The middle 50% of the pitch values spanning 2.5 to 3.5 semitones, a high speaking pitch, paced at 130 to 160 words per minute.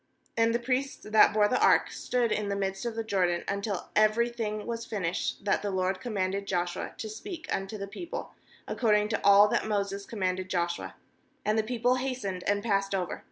No: average, 2.9 semitones; high, 210 Hz; average, 195 wpm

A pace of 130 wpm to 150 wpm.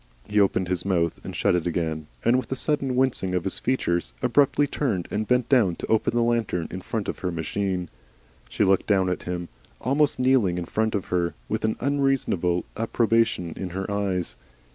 No: average, 195 wpm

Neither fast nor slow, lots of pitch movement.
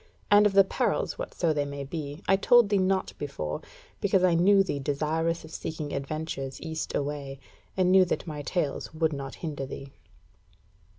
No: average, 175 wpm; average, 4.7 semitones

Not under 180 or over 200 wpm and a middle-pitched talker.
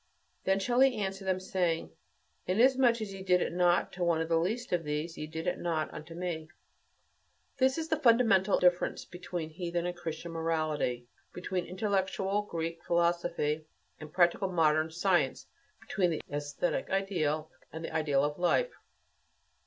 No: average, 160 wpm; medium, 175 Hz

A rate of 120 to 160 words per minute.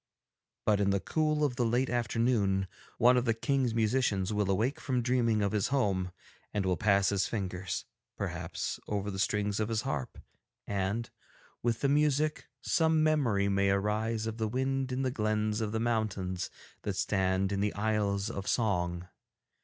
No: average, 170 wpm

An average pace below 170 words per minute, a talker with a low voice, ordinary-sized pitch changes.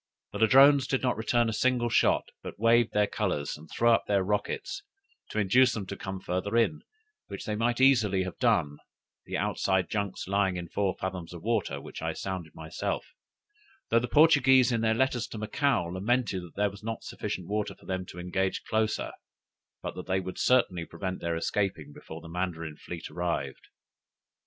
No: average, 180 wpm; low, 100 Hz; average, 4.4 semitones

